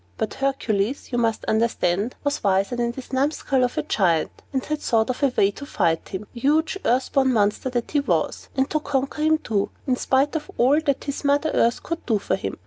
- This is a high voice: Yes, very high, 255 Hz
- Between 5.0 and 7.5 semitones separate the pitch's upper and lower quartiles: No, average, 4.4 semitones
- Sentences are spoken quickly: Yes, fast, 220 wpm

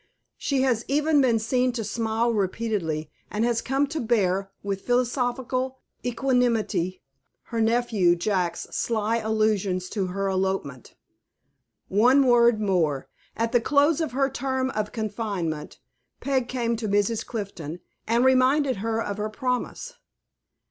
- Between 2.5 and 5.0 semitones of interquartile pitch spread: Yes, average, 4.3 semitones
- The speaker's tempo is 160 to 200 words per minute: No, slow, 135 wpm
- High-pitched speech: Yes, high, 225 Hz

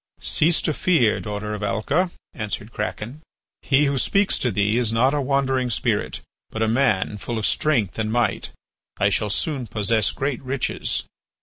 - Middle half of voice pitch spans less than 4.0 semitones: No, average, 4.6 semitones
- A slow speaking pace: No, average, 170 wpm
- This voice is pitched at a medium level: No, low, 115 Hz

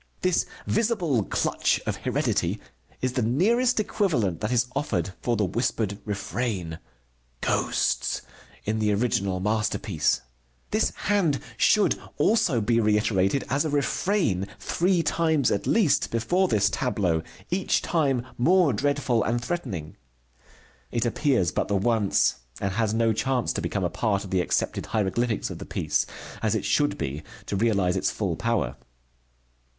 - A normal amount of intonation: No, wide, 6.5 semitones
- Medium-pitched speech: No, low, 115 Hz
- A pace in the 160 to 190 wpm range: No, average, 145 wpm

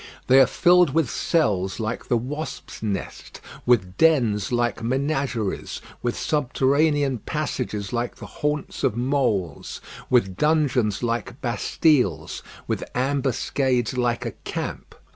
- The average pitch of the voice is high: No, low, 125 Hz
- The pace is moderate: No, slow, 120 wpm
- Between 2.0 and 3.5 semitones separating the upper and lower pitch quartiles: No, average, 4.0 semitones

